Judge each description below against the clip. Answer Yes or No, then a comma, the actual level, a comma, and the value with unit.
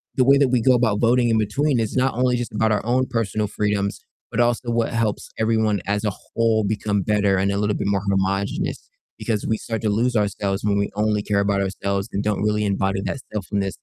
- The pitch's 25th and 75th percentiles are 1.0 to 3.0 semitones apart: Yes, narrow, 2.4 semitones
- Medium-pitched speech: No, low, 105 Hz